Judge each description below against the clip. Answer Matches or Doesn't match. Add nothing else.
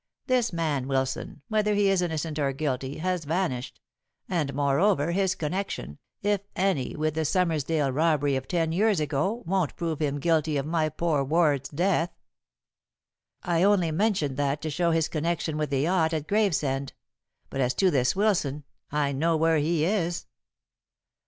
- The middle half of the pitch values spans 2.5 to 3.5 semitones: Doesn't match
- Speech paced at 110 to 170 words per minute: Matches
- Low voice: Doesn't match